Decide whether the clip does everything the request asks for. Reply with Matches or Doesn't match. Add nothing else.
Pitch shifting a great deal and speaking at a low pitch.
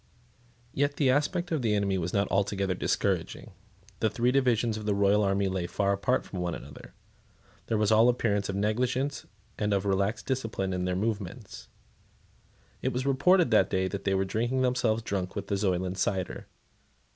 Doesn't match